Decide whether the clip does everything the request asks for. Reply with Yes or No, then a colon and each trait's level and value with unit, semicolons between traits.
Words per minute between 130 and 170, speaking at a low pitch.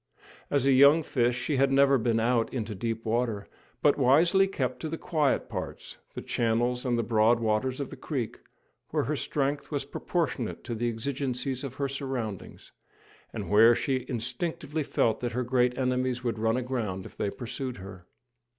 No: average, 180 wpm; low, 125 Hz